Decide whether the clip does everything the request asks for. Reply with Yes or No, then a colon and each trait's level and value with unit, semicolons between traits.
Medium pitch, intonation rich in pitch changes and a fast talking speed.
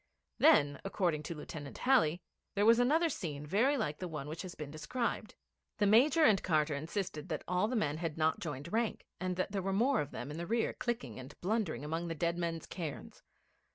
Yes: medium, 175 Hz; wide, 6.0 semitones; fast, 210 wpm